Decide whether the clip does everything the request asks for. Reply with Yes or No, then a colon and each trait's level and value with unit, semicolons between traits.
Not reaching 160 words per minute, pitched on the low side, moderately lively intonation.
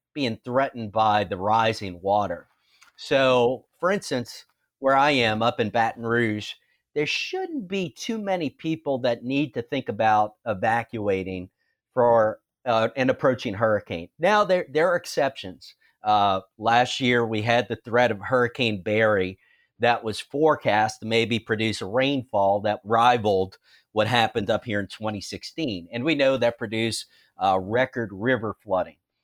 Yes: average, 150 wpm; low, 115 Hz; average, 4.0 semitones